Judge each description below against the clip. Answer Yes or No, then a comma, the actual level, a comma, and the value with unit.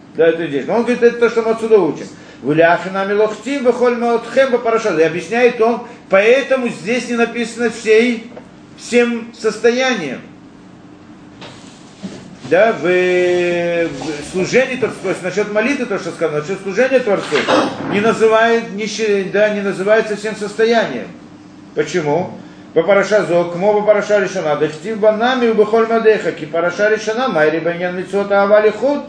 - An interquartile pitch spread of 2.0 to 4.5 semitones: Yes, average, 4.1 semitones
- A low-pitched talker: No, high, 215 Hz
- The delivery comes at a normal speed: Yes, average, 125 wpm